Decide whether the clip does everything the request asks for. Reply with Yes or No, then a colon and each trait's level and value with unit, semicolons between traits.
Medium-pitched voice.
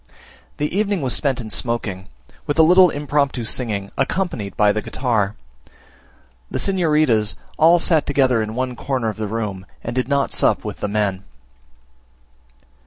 No: low, 125 Hz